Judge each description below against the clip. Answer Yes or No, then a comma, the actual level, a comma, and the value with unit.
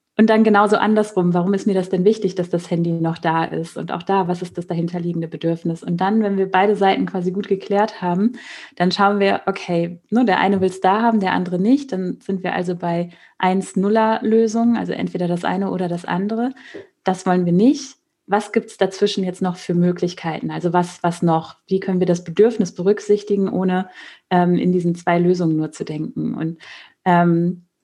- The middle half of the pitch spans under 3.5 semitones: Yes, average, 2.7 semitones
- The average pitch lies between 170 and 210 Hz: Yes, medium, 185 Hz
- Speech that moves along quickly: Yes, fast, 205 wpm